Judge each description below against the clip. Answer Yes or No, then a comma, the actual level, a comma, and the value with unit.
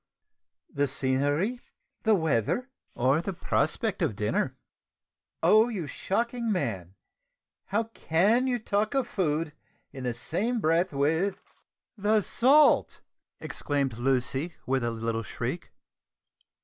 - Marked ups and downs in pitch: Yes, wide, 8.4 semitones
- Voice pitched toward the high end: No, medium, 165 Hz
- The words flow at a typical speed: No, slow, 125 wpm